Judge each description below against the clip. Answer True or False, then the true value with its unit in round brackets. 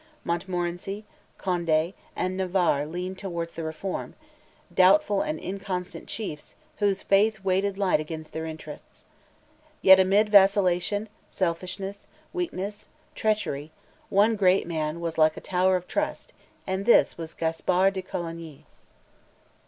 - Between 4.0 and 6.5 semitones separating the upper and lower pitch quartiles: False (2.8 semitones)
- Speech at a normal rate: False (120 wpm)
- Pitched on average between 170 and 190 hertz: True (185 Hz)